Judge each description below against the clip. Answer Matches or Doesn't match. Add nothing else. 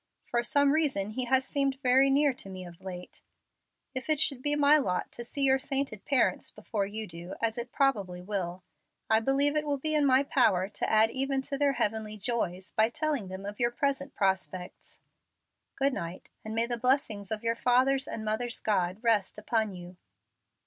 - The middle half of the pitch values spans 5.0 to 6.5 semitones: Matches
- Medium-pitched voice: Doesn't match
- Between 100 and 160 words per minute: Doesn't match